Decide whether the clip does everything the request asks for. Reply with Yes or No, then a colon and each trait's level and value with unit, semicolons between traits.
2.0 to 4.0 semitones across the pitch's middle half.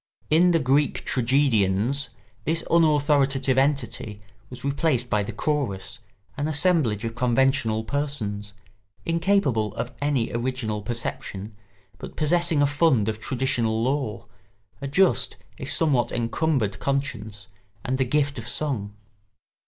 No: average, 4.7 semitones